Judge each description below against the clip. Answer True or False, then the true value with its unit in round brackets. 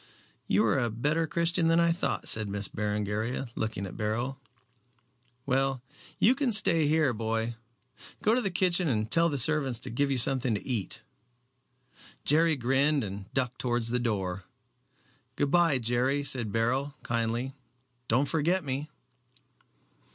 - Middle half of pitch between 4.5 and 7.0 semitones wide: True (5.2 semitones)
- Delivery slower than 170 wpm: True (150 wpm)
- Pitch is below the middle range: True (130 Hz)